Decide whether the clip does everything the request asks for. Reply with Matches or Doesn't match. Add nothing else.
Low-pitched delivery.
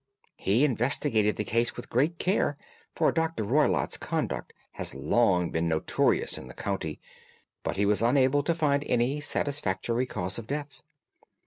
Matches